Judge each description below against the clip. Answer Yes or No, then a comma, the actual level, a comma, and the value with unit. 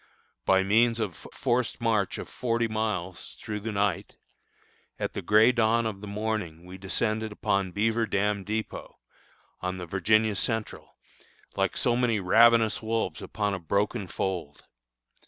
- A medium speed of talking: Yes, average, 150 wpm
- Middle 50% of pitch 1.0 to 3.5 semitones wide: Yes, average, 2.7 semitones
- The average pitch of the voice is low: Yes, low, 105 Hz